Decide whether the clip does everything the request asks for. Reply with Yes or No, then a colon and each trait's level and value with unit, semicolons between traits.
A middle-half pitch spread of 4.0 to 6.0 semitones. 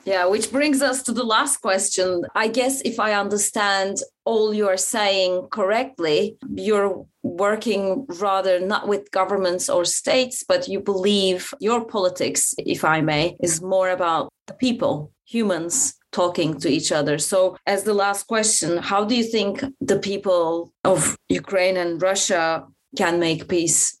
No: average, 3.4 semitones